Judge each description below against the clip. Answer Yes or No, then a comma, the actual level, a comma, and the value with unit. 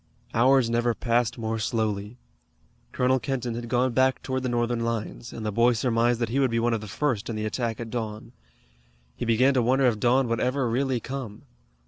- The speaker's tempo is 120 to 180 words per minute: No, fast, 205 wpm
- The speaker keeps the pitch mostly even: Yes, narrow, 2.1 semitones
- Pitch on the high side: No, low, 120 Hz